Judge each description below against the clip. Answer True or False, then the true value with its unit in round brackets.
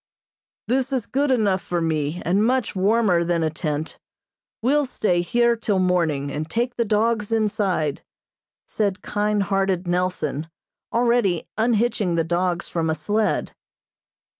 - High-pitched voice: True (195 Hz)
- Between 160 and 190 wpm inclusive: False (140 wpm)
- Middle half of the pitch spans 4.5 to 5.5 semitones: True (5.0 semitones)